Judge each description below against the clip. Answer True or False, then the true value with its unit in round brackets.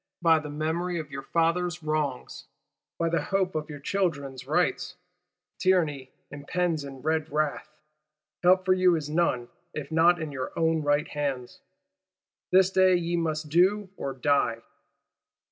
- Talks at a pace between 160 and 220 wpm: False (145 wpm)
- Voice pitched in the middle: True (160 Hz)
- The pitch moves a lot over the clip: False (3.4 semitones)